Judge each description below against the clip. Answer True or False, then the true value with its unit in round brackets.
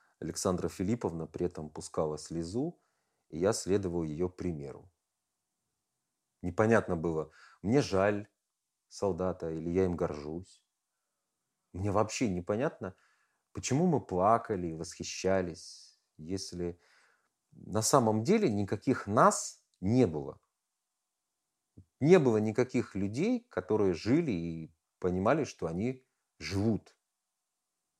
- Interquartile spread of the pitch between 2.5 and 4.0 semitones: False (4.5 semitones)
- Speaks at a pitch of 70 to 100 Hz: True (95 Hz)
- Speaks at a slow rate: True (100 wpm)